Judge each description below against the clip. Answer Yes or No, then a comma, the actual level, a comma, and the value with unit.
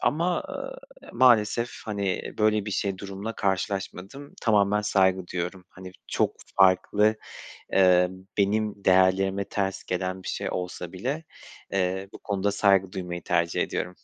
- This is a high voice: No, low, 100 Hz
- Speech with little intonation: Yes, narrow, 2.3 semitones